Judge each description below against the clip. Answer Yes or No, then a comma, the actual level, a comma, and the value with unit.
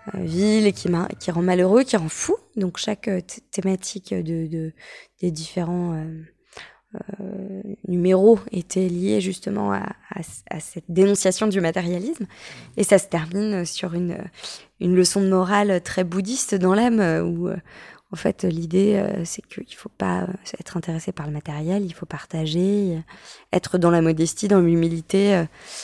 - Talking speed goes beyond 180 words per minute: No, average, 150 wpm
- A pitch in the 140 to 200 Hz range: Yes, medium, 185 Hz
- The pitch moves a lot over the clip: No, narrow, 2.6 semitones